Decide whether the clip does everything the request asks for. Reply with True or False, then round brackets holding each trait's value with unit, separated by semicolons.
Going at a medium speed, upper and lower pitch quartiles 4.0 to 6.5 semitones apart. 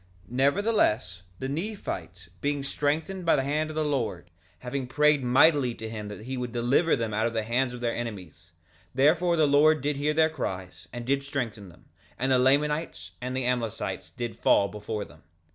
True (195 wpm; 5.0 semitones)